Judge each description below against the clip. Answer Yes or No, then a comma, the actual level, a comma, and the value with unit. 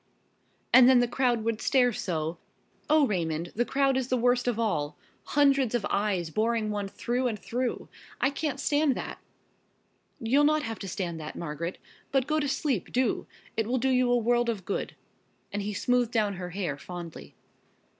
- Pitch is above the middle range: Yes, high, 235 Hz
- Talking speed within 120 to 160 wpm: No, average, 185 wpm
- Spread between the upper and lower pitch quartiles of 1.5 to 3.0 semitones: No, average, 4.8 semitones